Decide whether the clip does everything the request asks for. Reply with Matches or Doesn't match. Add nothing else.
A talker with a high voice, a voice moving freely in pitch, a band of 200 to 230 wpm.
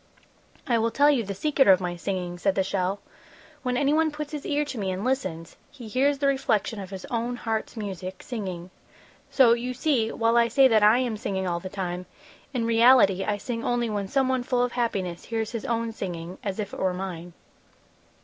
Doesn't match